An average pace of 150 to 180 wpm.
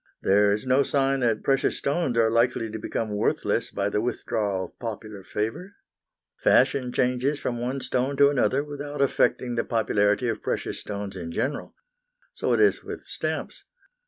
Yes: average, 165 wpm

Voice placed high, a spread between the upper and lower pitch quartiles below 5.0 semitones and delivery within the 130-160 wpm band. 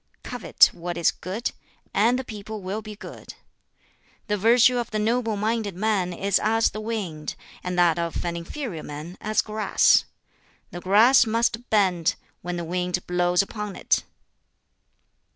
Yes: high, 205 Hz; average, 3.8 semitones; average, 150 wpm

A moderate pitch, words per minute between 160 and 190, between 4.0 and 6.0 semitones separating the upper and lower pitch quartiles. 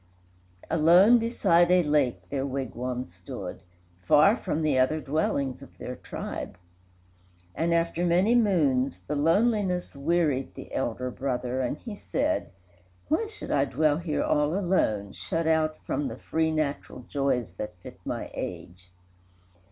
No: medium, 150 Hz; average, 140 wpm; average, 5.1 semitones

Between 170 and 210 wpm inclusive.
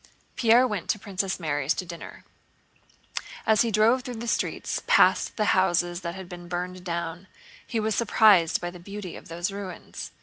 Yes: average, 175 wpm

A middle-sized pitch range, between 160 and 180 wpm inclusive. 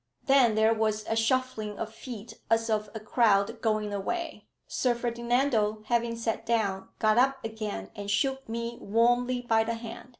No: narrow, 2.0 semitones; average, 165 wpm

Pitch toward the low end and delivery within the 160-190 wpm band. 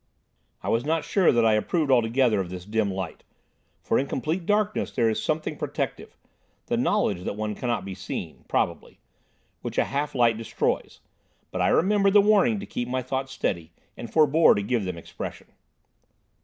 Yes: low, 125 Hz; average, 170 wpm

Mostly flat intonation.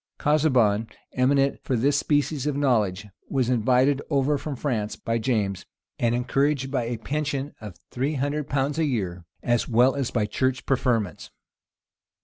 No: average, 3.7 semitones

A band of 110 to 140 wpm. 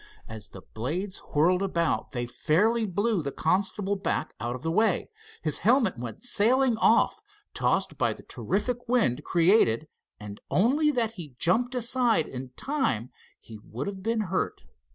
No: average, 155 wpm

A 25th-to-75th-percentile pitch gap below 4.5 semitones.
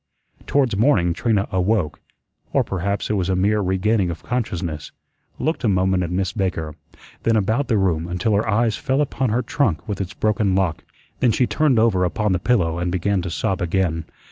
Yes: average, 3.7 semitones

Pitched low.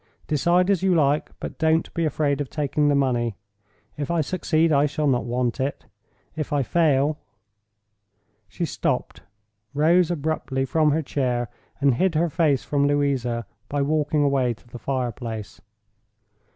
No: medium, 145 Hz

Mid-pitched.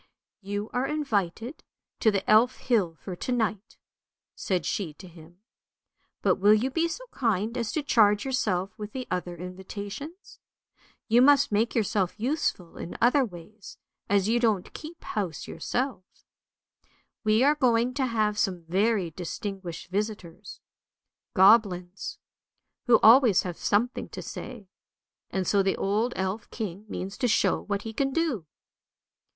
No: high, 210 Hz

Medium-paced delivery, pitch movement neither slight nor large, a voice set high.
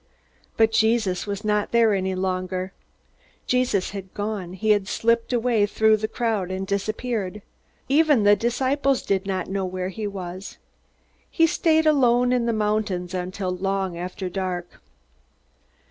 Yes: average, 145 wpm; average, 3.7 semitones; high, 205 Hz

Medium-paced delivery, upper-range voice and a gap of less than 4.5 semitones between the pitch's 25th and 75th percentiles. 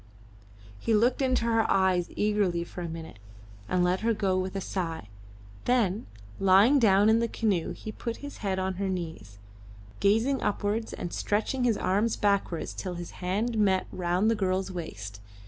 Yes: average, 170 wpm; high, 195 Hz; average, 3.6 semitones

